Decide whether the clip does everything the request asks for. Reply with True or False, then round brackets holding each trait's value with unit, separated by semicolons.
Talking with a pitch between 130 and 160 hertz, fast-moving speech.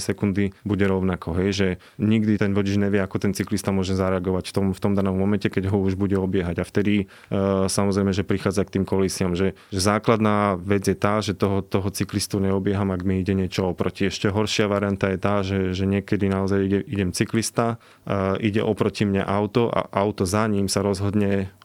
False (100 Hz; 200 wpm)